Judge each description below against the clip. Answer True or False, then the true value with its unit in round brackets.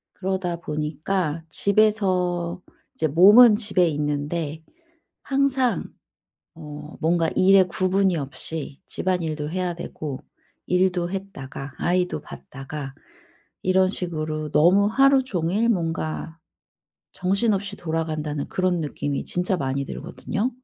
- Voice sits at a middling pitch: True (175 Hz)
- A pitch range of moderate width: True (3.8 semitones)